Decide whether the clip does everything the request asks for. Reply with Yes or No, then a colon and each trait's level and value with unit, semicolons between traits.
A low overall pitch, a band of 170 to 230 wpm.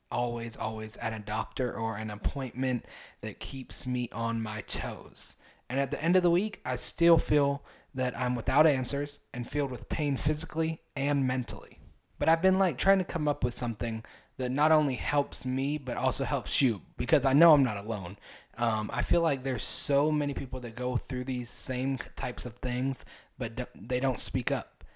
Yes: low, 130 Hz; average, 195 wpm